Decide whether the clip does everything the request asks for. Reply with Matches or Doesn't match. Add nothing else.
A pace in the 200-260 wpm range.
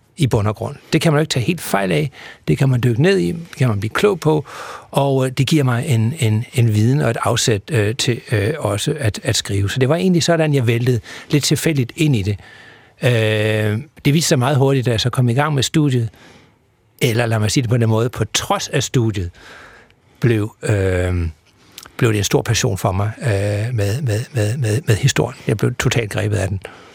Matches